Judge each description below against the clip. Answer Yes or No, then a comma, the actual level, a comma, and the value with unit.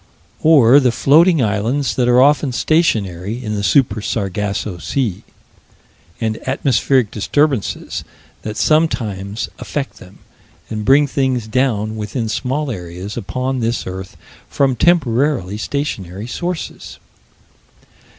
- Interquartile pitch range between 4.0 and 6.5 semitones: Yes, average, 5.1 semitones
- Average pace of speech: No, slow, 110 wpm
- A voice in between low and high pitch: No, low, 120 Hz